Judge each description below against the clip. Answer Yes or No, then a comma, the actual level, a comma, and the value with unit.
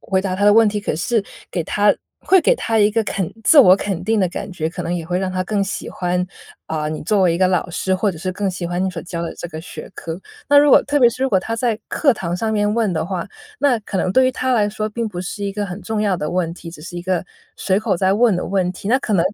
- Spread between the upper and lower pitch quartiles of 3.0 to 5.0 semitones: Yes, average, 3.4 semitones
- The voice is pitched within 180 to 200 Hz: Yes, high, 190 Hz